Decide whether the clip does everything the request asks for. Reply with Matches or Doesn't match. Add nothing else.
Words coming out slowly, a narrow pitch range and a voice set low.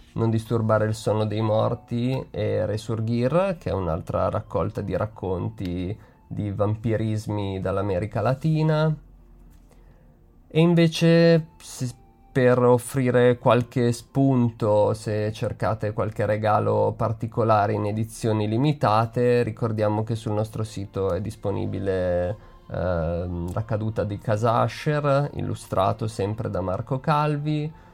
Doesn't match